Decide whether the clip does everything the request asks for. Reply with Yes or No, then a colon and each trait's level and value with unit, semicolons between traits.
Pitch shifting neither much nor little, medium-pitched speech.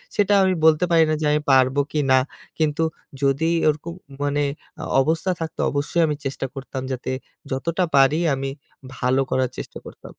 Yes: average, 3.3 semitones; medium, 145 Hz